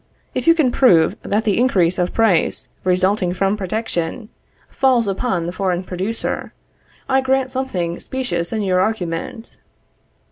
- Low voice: No, high, 200 Hz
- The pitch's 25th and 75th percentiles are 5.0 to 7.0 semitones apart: Yes, wide, 5.4 semitones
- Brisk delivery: No, average, 140 wpm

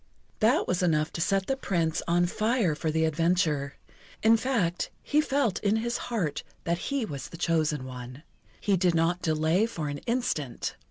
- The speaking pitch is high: No, medium, 175 Hz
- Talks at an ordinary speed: Yes, average, 175 wpm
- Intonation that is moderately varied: No, wide, 5.8 semitones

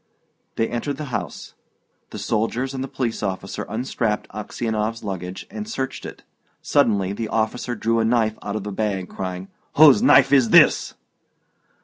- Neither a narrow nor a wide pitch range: Yes, average, 3.5 semitones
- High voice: No, low, 110 Hz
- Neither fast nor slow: Yes, average, 155 wpm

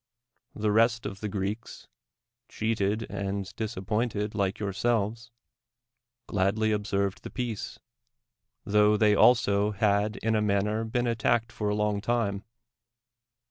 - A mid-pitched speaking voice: No, low, 105 Hz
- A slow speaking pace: Yes, slow, 125 wpm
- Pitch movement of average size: No, narrow, 1.9 semitones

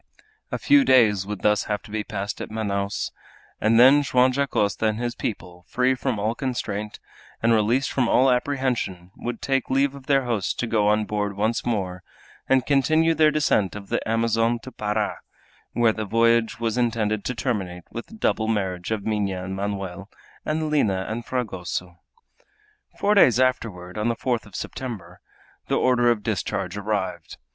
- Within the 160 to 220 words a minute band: Yes, average, 175 wpm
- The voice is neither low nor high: No, low, 110 Hz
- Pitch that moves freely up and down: No, average, 3.8 semitones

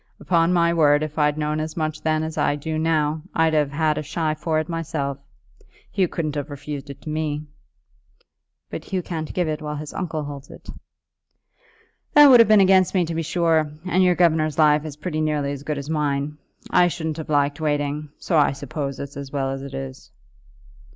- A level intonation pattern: Yes, narrow, 2.0 semitones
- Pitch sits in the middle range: Yes, medium, 155 Hz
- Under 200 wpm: No, fast, 205 wpm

